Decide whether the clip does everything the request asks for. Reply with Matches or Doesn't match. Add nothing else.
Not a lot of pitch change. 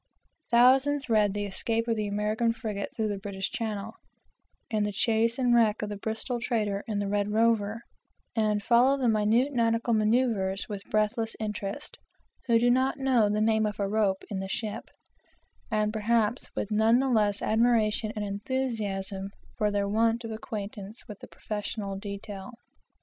Matches